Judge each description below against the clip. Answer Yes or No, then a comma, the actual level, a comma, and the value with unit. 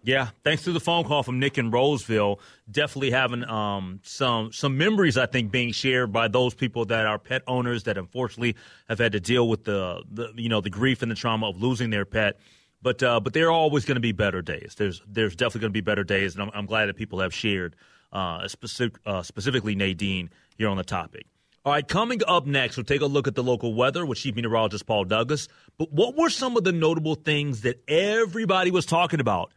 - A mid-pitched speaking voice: No, low, 120 Hz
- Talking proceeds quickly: Yes, fast, 235 wpm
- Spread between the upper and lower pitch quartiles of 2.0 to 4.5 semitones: No, average, 5.0 semitones